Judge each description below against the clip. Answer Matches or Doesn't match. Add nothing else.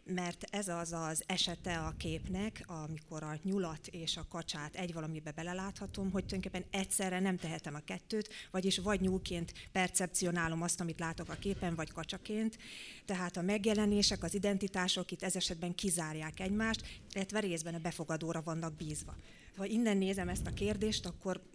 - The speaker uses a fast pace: Matches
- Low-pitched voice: Doesn't match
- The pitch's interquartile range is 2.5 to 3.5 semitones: Matches